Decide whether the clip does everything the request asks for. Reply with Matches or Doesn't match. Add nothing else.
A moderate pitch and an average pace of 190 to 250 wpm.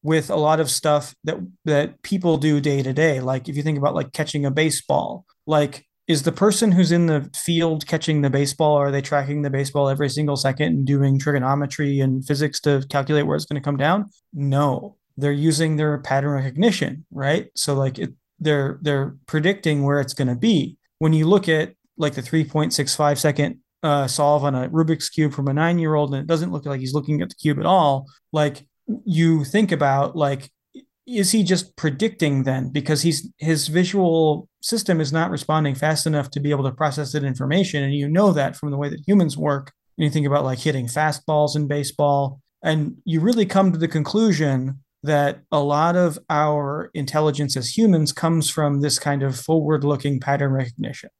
Matches